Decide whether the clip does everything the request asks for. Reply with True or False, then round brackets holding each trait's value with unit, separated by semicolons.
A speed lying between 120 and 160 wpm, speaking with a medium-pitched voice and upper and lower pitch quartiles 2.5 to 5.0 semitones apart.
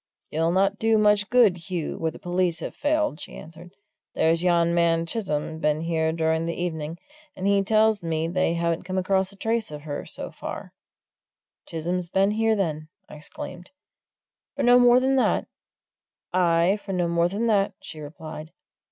False (175 wpm; 175 Hz; 3.7 semitones)